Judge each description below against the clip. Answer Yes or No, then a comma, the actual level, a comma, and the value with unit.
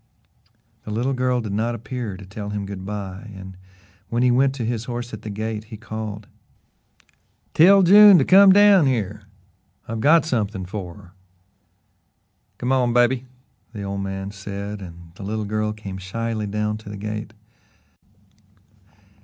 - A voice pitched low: Yes, low, 110 Hz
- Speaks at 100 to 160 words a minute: Yes, average, 155 wpm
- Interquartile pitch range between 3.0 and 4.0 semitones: Yes, average, 3.4 semitones